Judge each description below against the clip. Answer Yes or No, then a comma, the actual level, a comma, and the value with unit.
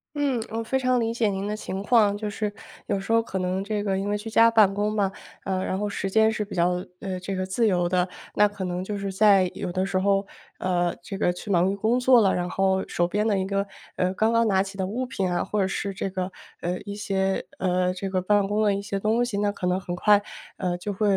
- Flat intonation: Yes, narrow, 2.1 semitones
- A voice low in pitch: No, high, 195 Hz